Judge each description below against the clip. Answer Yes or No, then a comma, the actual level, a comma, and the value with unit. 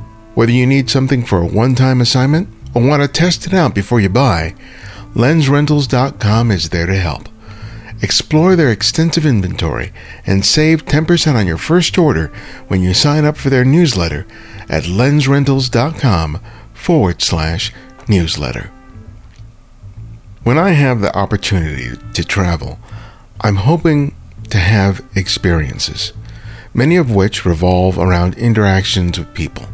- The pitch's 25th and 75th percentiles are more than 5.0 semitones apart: Yes, wide, 5.5 semitones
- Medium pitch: No, low, 110 Hz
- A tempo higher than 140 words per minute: No, slow, 135 wpm